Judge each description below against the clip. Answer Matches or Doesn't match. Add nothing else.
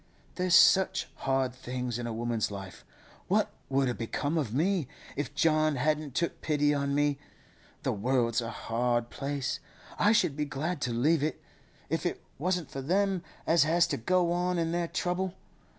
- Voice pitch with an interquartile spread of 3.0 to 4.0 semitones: Doesn't match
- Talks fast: Doesn't match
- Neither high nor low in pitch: Matches